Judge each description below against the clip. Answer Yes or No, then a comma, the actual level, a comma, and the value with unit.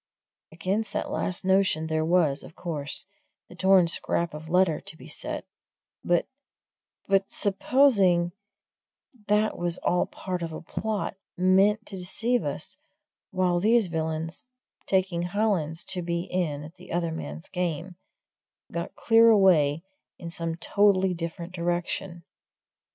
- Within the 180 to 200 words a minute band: No, slow, 135 wpm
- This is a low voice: No, medium, 175 Hz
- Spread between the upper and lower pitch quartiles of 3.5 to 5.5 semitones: No, narrow, 2.6 semitones